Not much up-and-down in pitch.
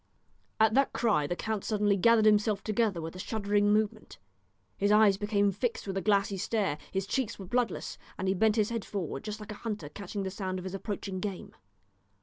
Yes: narrow, 2.1 semitones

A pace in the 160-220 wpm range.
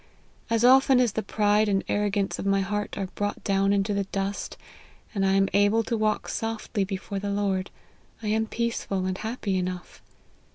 Yes: average, 180 wpm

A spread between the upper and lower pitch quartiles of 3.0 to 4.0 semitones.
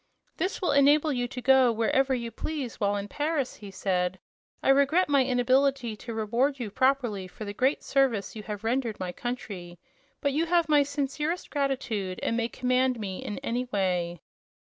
No: average, 4.7 semitones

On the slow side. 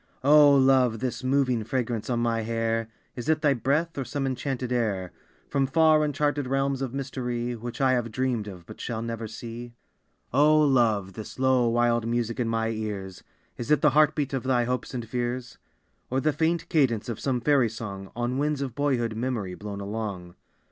No: average, 190 wpm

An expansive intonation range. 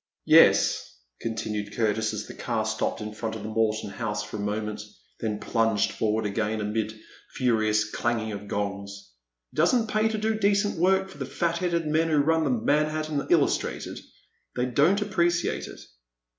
Yes: wide, 7.5 semitones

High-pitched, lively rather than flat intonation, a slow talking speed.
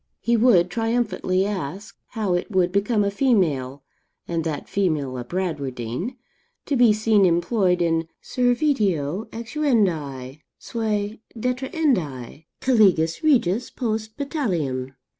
Yes: high, 200 Hz; wide, 6.3 semitones; slow, 110 wpm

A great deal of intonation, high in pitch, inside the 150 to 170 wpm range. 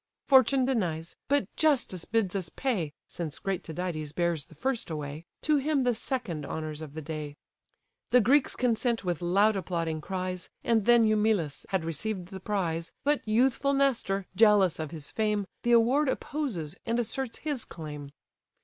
Yes: wide, 6.7 semitones; high, 195 Hz; average, 160 wpm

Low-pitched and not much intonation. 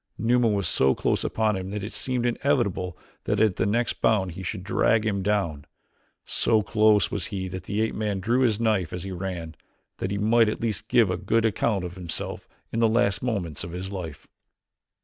No: low, 100 Hz; average, 3.3 semitones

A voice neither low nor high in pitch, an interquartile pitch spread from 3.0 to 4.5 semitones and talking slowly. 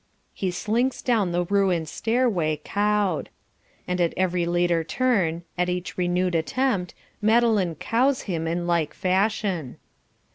Yes: medium, 180 Hz; average, 3.8 semitones; slow, 130 wpm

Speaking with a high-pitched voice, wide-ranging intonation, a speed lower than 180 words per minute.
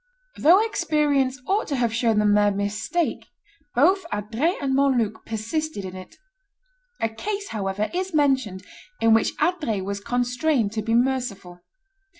Yes: high, 245 Hz; wide, 6.4 semitones; average, 145 wpm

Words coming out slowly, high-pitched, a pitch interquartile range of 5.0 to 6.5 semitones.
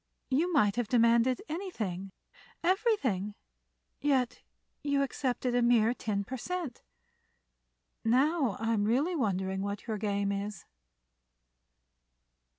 Yes: slow, 95 wpm; high, 235 Hz; wide, 5.5 semitones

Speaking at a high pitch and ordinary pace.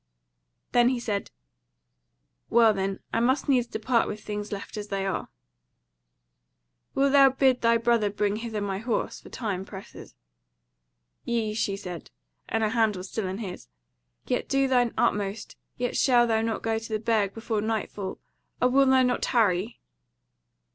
Yes: high, 225 Hz; average, 160 wpm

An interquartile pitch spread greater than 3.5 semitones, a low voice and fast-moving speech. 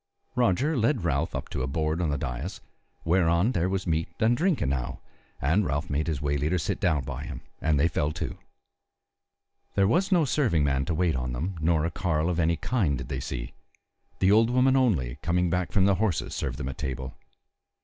Yes: wide, 5.4 semitones; very low, 80 Hz; fast, 210 wpm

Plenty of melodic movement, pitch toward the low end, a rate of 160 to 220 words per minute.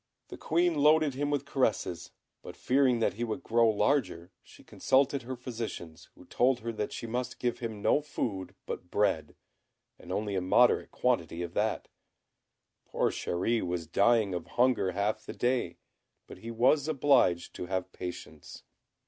Yes: wide, 5.8 semitones; low, 115 Hz; average, 165 wpm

